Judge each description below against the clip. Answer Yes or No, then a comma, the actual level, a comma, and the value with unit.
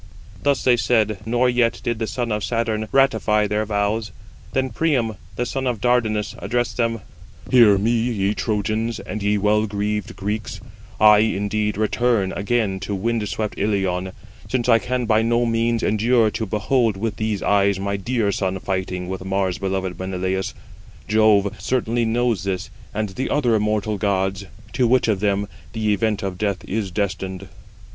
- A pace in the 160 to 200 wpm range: Yes, average, 165 wpm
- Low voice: Yes, low, 105 Hz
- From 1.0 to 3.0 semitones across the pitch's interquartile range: Yes, average, 2.7 semitones